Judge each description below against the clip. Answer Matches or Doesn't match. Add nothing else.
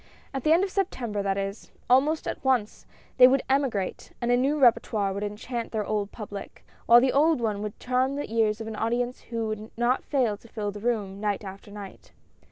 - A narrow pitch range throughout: Doesn't match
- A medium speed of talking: Doesn't match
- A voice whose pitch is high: Matches